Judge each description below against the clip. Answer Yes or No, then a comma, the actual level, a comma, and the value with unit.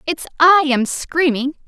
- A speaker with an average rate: Yes, average, 145 wpm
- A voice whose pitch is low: No, very high, 300 Hz